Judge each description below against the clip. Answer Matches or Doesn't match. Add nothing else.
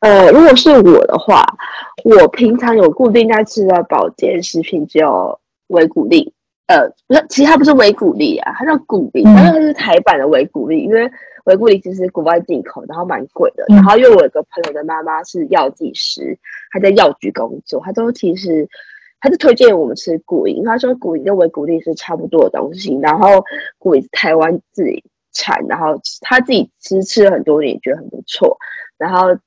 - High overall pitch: Matches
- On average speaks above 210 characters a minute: Matches